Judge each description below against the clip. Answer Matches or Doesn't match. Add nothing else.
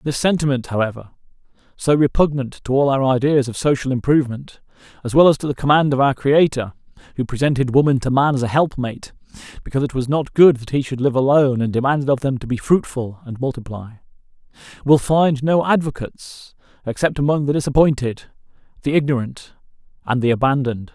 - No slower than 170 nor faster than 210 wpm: Matches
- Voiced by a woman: Doesn't match